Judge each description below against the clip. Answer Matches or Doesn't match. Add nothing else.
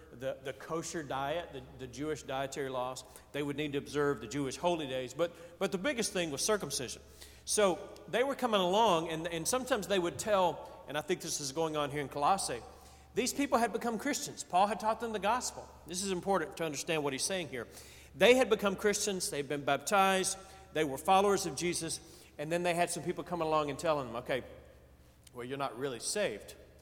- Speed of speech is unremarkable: Doesn't match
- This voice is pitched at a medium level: Matches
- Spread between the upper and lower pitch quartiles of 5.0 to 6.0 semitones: Matches